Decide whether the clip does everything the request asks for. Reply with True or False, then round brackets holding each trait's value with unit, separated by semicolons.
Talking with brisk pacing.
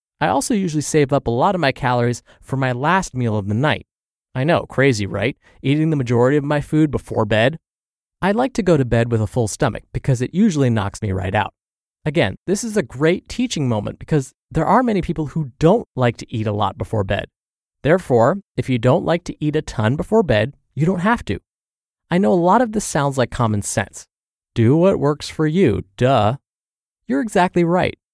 True (215 wpm)